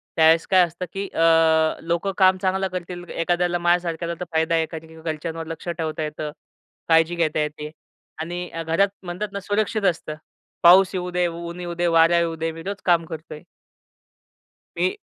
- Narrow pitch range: Yes, narrow, 1.7 semitones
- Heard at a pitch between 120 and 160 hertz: No, medium, 170 Hz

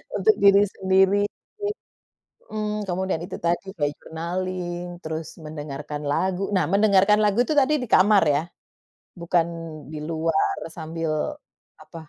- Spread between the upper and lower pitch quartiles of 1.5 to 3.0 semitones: No, average, 3.7 semitones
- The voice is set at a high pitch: No, medium, 180 Hz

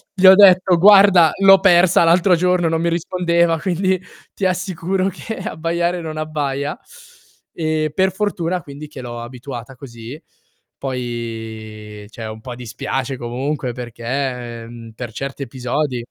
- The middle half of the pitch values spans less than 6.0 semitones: No, wide, 6.6 semitones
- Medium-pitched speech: Yes, medium, 150 Hz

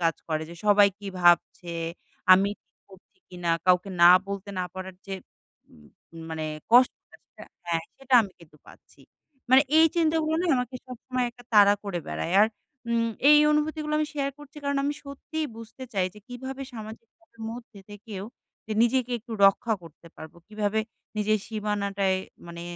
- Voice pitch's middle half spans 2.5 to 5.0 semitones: No, wide, 5.6 semitones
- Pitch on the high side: Yes, high, 215 Hz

